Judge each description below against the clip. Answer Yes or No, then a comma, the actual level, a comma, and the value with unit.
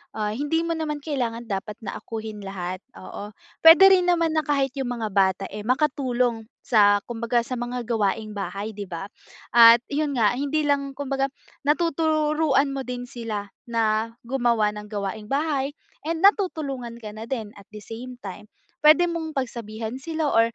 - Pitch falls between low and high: No, high, 240 Hz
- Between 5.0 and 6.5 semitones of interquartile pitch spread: Yes, average, 5.3 semitones